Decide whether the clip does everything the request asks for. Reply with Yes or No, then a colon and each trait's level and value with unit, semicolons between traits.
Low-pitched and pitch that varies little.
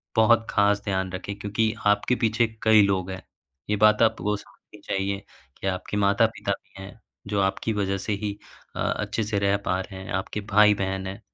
Yes: low, 100 Hz; narrow, 1.8 semitones